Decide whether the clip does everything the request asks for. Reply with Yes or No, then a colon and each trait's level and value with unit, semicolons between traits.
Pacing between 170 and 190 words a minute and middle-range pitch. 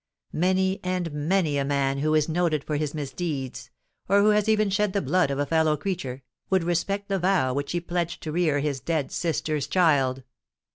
Yes: average, 185 wpm; medium, 160 Hz